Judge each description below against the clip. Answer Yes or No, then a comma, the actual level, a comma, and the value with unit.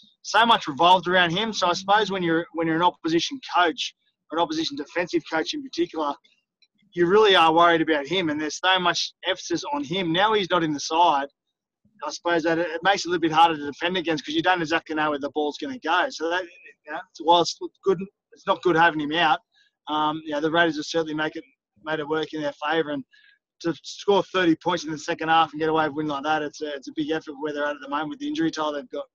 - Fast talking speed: Yes, fast, 260 wpm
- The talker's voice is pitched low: No, medium, 170 Hz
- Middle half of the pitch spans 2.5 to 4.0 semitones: Yes, average, 3.5 semitones